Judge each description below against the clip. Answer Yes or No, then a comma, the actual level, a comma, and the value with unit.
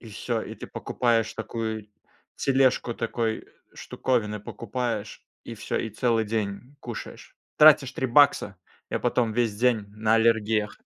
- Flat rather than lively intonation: Yes, narrow, 2.2 semitones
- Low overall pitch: Yes, low, 115 Hz